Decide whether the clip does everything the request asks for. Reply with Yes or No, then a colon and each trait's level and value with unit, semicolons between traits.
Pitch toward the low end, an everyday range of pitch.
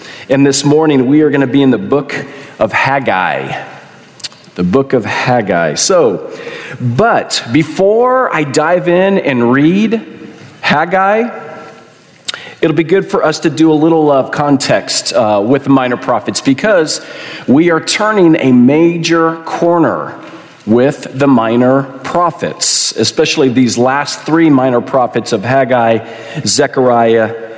No: medium, 145 Hz; average, 4.4 semitones